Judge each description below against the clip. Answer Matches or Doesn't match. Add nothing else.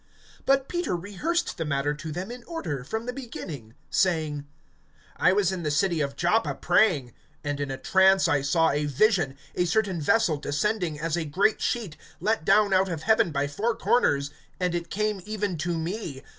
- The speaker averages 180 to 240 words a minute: Matches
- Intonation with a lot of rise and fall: Matches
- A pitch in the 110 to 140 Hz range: Doesn't match